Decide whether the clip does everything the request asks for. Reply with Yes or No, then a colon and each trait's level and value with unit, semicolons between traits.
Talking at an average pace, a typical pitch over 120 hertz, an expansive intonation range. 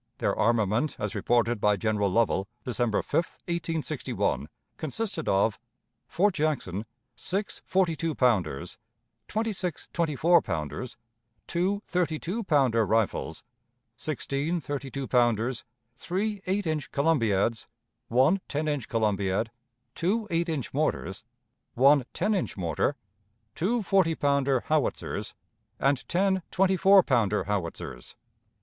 No: slow, 120 wpm; medium, 140 Hz; wide, 7.4 semitones